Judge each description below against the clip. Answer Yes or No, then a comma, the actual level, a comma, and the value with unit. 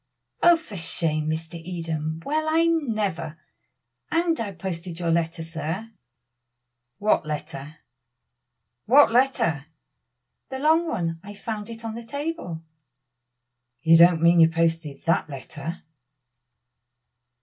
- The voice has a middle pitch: Yes, medium, 170 Hz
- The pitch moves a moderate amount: No, wide, 6.0 semitones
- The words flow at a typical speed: No, slow, 115 wpm